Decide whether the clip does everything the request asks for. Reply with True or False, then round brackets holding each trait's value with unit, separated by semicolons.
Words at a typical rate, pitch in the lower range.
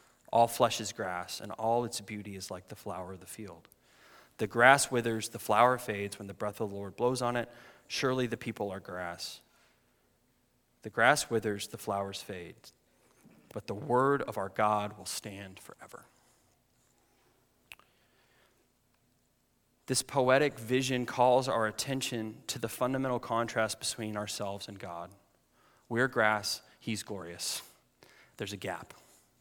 True (145 wpm; 110 Hz)